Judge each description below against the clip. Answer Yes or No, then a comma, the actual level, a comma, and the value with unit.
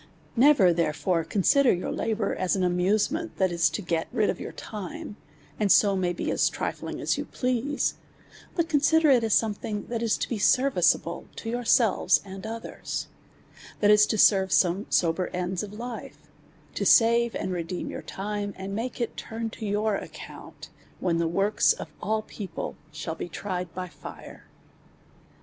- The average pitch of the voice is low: No, high, 205 Hz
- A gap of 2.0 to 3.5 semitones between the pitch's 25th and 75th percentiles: No, average, 4.1 semitones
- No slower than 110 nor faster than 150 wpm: No, average, 170 wpm